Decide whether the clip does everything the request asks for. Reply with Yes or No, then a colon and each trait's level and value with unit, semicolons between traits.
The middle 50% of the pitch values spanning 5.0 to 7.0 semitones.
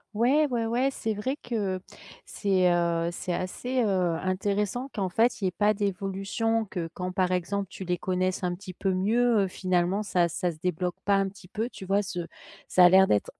No: average, 2.9 semitones